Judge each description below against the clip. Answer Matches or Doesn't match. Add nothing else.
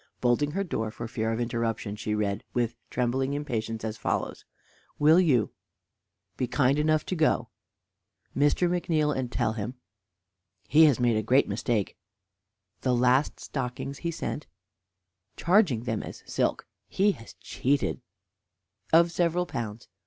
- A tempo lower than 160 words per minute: Matches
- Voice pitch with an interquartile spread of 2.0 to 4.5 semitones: Doesn't match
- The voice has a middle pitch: Doesn't match